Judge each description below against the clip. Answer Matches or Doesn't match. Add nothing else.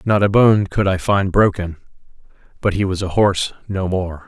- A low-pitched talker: Matches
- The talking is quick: Doesn't match